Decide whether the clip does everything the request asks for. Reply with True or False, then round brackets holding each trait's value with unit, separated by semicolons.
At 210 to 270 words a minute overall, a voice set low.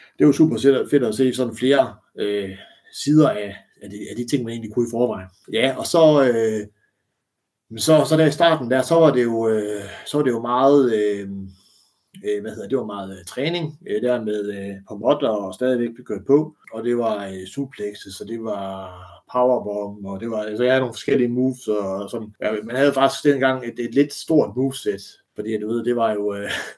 True (220 wpm; 120 Hz)